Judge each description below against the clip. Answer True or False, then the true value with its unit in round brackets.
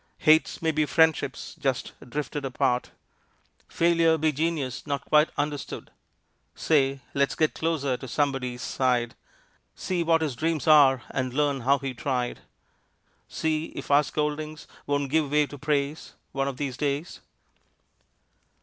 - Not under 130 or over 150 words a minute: True (140 wpm)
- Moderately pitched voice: True (145 Hz)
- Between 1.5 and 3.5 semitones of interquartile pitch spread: True (2.5 semitones)